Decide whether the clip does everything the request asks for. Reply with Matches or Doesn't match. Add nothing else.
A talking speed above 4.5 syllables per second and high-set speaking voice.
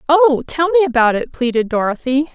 Matches